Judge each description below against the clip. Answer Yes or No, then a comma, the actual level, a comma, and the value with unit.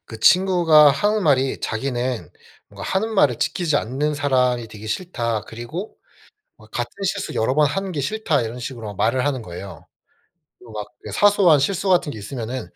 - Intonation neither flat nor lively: No, wide, 6.9 semitones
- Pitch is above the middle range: No, low, 135 Hz